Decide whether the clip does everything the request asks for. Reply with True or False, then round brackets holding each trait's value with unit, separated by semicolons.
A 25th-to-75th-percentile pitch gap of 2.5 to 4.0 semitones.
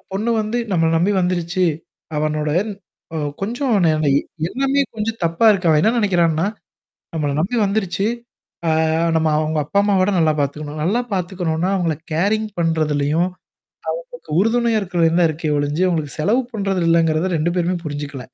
False (4.4 semitones)